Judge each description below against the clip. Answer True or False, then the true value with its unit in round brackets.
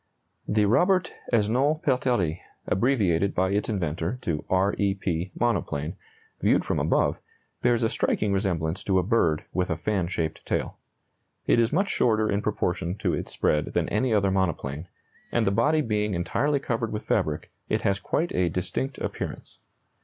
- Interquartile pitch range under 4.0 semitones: False (4.7 semitones)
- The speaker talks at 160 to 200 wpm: True (165 wpm)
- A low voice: True (100 Hz)